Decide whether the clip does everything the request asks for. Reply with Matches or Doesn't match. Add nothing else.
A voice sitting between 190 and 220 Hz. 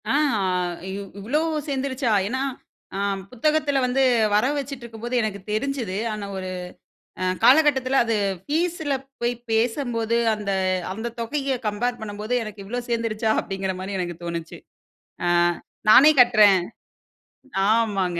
Doesn't match